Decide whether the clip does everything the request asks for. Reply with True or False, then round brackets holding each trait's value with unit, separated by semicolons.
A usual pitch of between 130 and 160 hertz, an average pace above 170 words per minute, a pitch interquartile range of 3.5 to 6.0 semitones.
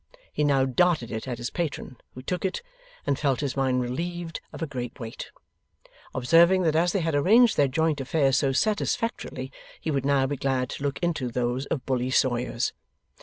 True (140 Hz; 190 wpm; 4.3 semitones)